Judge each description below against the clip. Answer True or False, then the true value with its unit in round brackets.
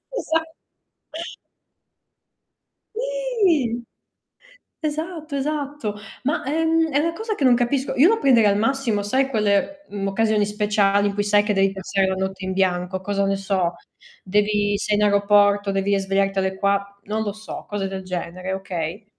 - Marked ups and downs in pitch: True (5.8 semitones)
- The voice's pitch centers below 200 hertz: False (205 Hz)